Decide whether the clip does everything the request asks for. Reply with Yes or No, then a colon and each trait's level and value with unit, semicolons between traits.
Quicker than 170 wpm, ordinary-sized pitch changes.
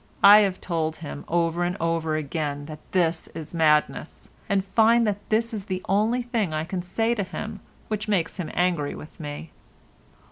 Yes: average, 180 wpm; average, 4.6 semitones